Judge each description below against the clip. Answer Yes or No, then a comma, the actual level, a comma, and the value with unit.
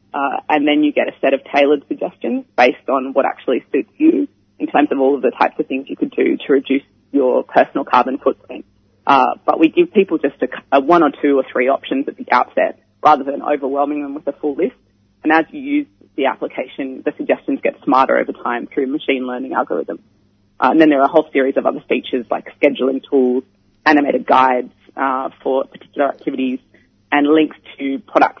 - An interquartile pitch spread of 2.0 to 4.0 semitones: Yes, average, 2.9 semitones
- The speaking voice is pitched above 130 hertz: Yes, medium, 140 Hz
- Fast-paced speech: Yes, fast, 210 wpm